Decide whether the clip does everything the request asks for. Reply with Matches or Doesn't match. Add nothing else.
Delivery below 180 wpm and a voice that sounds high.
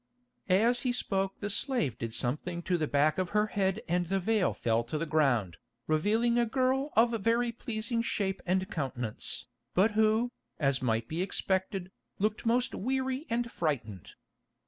Matches